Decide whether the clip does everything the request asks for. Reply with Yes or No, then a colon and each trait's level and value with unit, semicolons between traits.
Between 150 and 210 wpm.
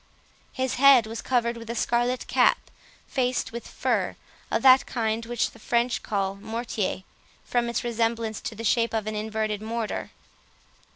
Yes: average, 155 wpm